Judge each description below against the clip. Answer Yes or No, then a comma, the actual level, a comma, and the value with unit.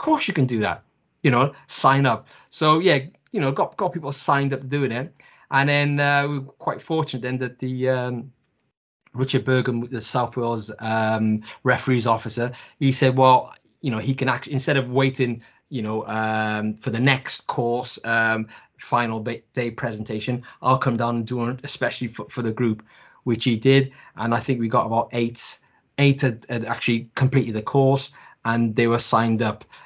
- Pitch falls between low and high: No, low, 125 Hz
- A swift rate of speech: No, average, 190 wpm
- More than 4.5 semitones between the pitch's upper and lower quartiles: No, average, 2.7 semitones